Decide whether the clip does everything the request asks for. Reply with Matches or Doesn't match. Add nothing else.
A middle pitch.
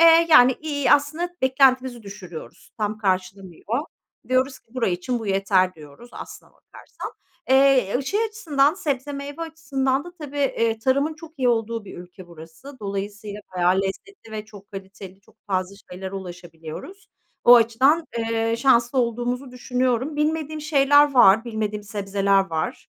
Doesn't match